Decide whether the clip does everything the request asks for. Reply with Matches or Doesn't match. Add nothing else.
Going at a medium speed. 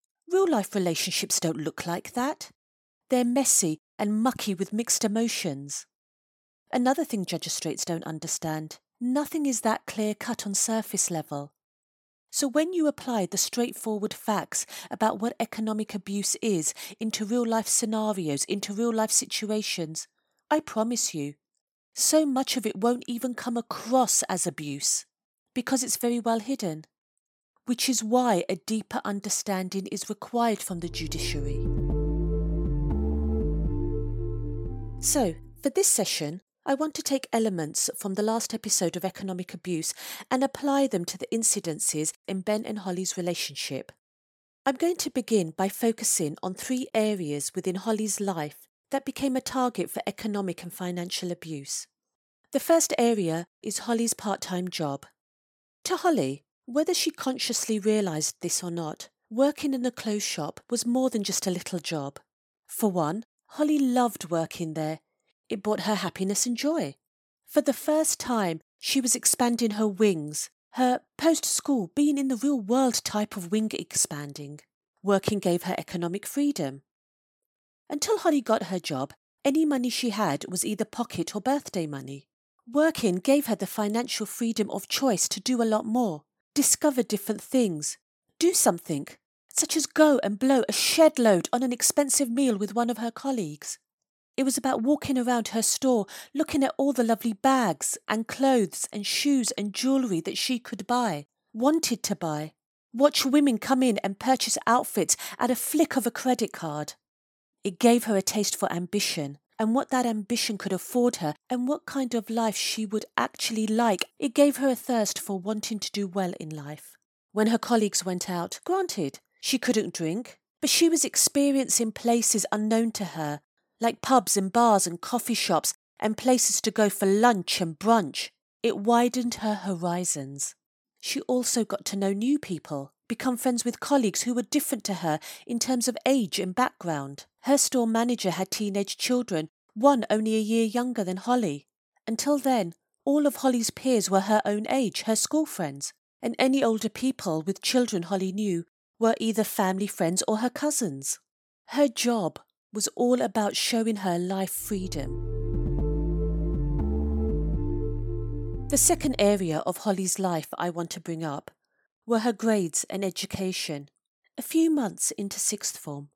Matches